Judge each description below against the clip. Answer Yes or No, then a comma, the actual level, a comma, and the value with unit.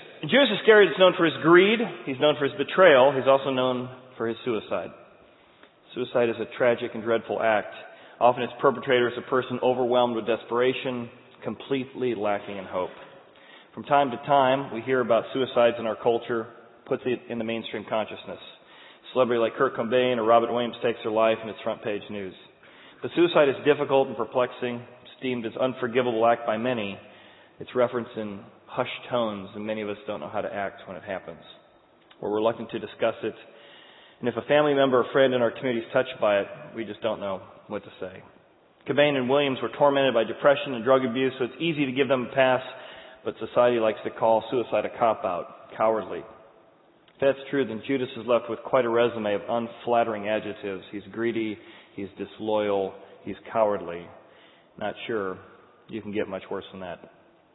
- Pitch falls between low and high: No, low, 120 Hz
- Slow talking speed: No, average, 195 wpm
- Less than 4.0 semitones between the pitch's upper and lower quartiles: Yes, average, 2.8 semitones